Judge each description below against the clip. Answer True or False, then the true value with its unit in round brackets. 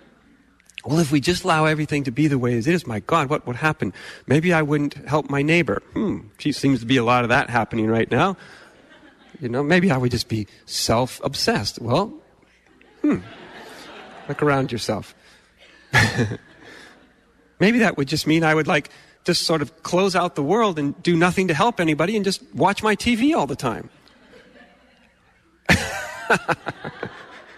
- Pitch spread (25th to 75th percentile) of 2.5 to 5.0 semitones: True (4.7 semitones)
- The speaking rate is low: False (170 wpm)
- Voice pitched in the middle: True (155 Hz)